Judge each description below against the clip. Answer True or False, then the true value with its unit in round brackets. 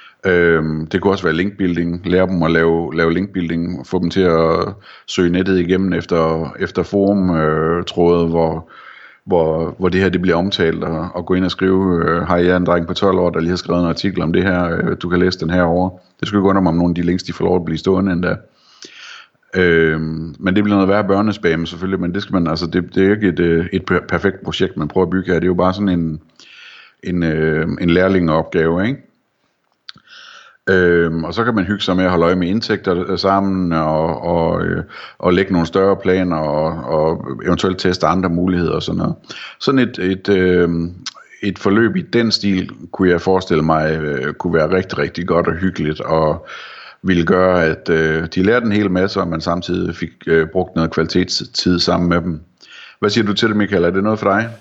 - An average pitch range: False (2.2 semitones)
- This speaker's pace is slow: False (210 wpm)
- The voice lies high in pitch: False (90 Hz)